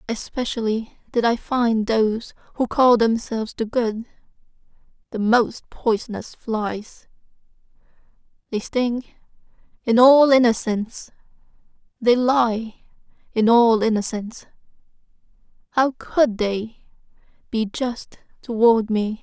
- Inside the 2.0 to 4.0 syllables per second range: Yes, 3.9 syllables/s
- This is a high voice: Yes, high, 230 Hz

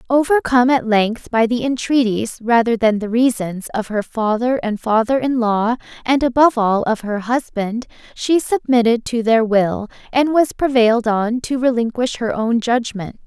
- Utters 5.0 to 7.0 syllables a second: No, 4.6 syllables/s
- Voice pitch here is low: No, high, 235 Hz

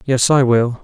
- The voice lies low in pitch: Yes, low, 125 Hz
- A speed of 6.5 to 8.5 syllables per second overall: No, 4.1 syllables/s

